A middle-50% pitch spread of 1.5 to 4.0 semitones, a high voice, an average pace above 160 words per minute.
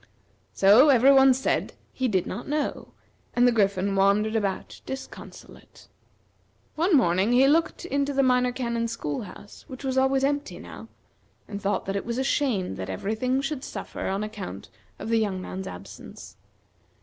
No: average, 5.1 semitones; high, 235 Hz; average, 170 wpm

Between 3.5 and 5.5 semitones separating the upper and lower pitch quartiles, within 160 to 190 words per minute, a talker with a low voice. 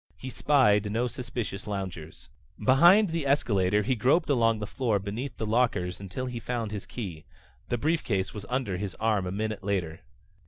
Yes: average, 4.3 semitones; average, 170 wpm; low, 110 Hz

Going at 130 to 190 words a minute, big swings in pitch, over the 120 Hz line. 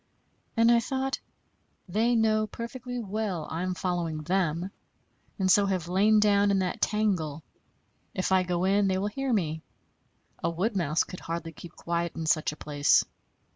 No: average, 170 wpm; average, 4.2 semitones; high, 190 Hz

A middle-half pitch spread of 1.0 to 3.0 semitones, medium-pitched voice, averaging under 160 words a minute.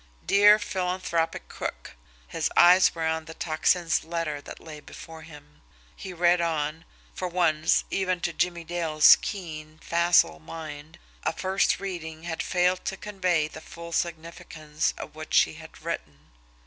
Yes: narrow, 2.4 semitones; medium, 165 Hz; average, 150 wpm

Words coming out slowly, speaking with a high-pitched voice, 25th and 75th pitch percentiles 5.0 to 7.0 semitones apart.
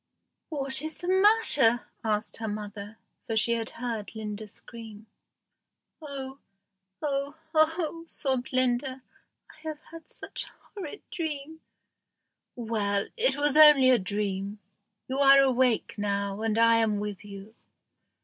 Yes: slow, 130 wpm; high, 245 Hz; wide, 5.5 semitones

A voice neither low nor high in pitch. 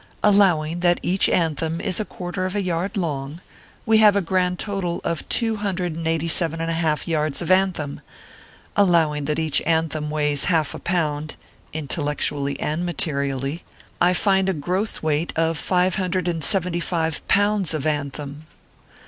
Yes: medium, 165 Hz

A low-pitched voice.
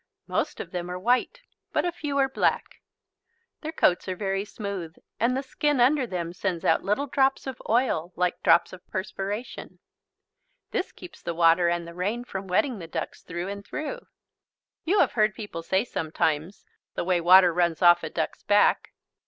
No: high, 195 Hz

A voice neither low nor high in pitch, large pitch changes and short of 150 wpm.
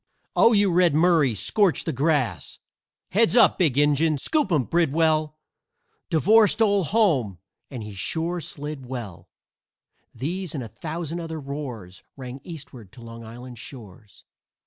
Yes: medium, 150 Hz; wide, 5.9 semitones; average, 140 wpm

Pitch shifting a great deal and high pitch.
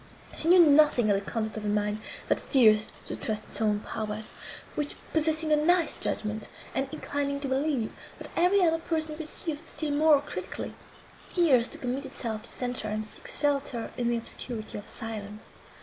Yes: wide, 6.1 semitones; very high, 265 Hz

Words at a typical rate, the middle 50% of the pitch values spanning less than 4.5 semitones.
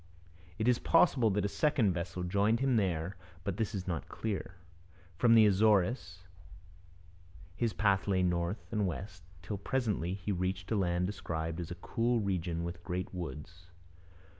Yes: average, 160 wpm; average, 3.6 semitones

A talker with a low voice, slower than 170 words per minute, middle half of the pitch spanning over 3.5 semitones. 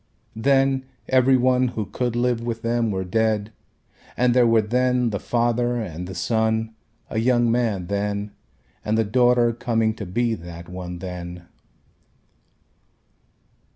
No: low, 115 Hz; average, 140 wpm; average, 3.2 semitones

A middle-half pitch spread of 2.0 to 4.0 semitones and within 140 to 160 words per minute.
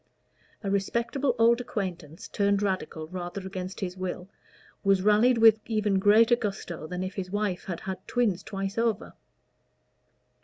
Yes: average, 3.0 semitones; average, 145 wpm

